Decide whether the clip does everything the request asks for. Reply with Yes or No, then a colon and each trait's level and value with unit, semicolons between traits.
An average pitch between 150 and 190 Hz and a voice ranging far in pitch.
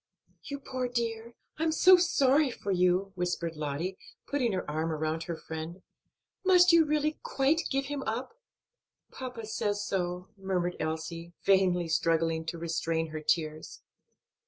Yes: medium, 185 Hz; wide, 7.9 semitones